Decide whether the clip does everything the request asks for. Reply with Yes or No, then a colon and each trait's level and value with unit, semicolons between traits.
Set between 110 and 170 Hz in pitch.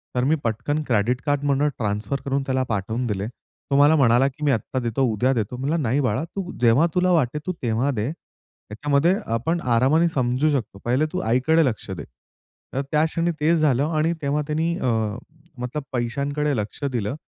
Yes: low, 135 Hz